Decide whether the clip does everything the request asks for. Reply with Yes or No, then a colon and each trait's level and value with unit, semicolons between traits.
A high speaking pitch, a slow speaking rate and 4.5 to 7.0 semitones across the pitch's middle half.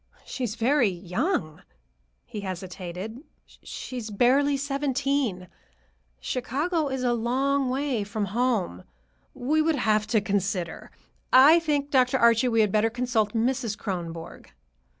Yes: high, 240 Hz; slow, 130 wpm; average, 5.1 semitones